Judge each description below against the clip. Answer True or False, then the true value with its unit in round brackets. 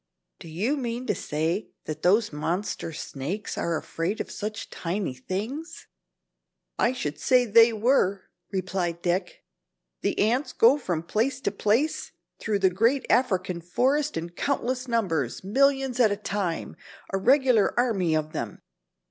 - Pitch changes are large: True (6.1 semitones)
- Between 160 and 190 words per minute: False (145 wpm)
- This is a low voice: False (205 Hz)